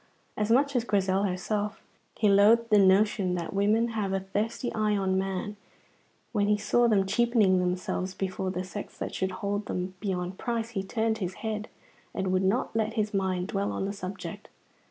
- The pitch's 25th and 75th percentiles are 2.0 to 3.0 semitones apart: Yes, narrow, 2.5 semitones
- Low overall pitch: No, high, 200 Hz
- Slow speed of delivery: No, average, 185 wpm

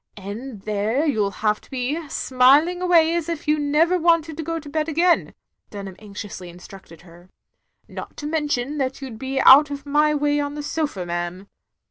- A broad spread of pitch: Yes, wide, 6.7 semitones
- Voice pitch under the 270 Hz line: No, very high, 285 Hz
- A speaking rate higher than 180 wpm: Yes, average, 195 wpm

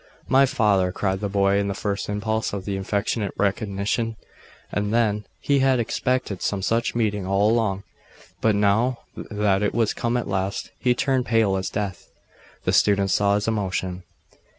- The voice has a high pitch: No, low, 105 Hz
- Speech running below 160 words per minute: No, average, 165 wpm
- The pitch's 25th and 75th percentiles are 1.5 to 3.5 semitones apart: Yes, narrow, 2.5 semitones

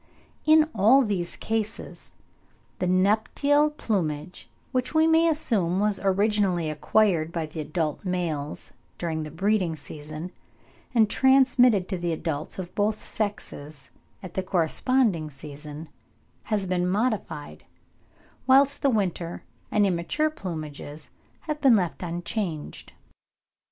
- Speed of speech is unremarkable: No, slow, 120 wpm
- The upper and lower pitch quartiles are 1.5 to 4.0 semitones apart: No, wide, 5.6 semitones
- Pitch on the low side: No, medium, 185 Hz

